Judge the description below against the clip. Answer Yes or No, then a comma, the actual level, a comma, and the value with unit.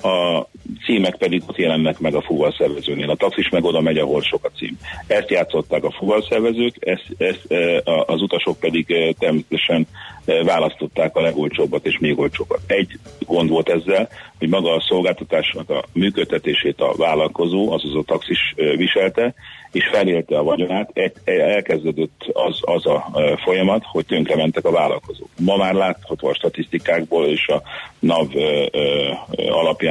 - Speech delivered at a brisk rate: Yes, fast, 165 wpm